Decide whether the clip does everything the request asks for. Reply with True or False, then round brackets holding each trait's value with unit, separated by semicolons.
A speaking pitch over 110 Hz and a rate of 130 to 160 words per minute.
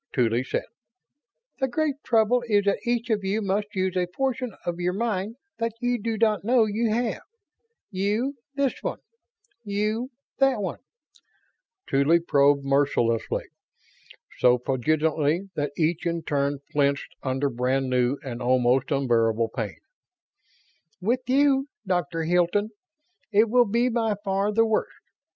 True (190 Hz; 135 wpm)